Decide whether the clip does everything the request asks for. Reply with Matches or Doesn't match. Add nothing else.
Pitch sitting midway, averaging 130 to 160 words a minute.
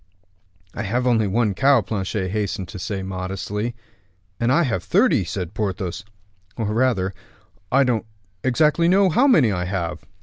Doesn't match